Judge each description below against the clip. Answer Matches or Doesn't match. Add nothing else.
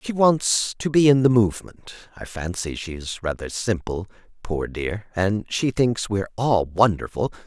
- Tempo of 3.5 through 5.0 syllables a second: Matches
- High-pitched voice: Doesn't match